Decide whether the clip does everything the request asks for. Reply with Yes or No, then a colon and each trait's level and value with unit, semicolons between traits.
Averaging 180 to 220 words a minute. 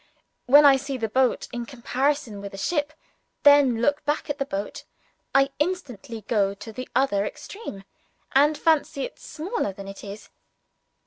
No: average, 170 wpm